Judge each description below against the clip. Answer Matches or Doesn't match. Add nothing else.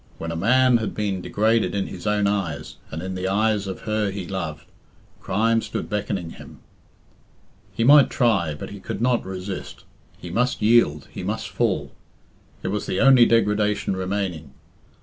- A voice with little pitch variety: Doesn't match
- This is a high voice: Doesn't match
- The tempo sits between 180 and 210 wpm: Doesn't match